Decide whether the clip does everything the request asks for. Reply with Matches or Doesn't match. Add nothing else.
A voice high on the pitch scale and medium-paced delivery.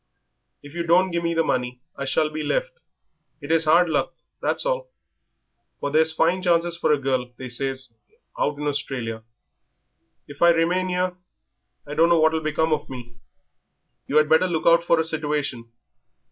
Doesn't match